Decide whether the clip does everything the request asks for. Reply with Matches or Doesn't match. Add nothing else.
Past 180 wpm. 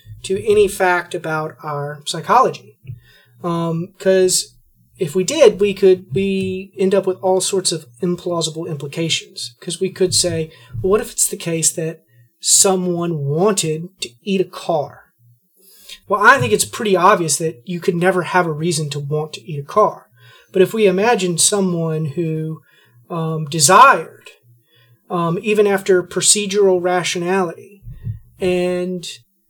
Doesn't match